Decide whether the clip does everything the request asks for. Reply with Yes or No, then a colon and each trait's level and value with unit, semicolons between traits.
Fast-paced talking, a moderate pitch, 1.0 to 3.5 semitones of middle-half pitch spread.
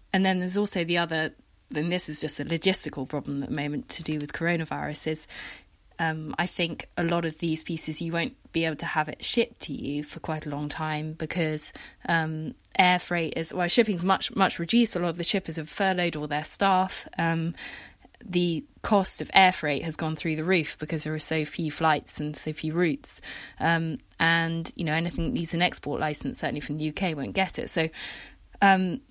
Yes: fast, 210 wpm; medium, 165 Hz; narrow, 2.4 semitones